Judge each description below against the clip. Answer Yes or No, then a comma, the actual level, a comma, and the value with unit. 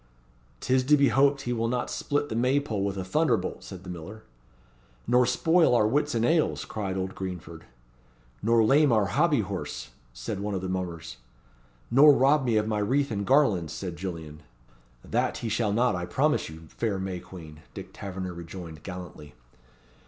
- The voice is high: No, low, 105 Hz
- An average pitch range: No, wide, 6.0 semitones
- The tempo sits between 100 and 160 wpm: No, average, 175 wpm